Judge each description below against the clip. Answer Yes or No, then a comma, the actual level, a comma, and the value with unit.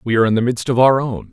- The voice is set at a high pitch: No, low, 120 Hz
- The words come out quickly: Yes, fast, 365 wpm